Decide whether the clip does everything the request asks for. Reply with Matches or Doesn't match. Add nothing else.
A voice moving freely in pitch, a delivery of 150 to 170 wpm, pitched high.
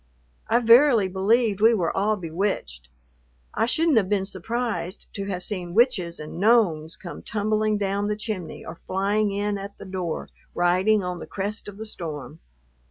Doesn't match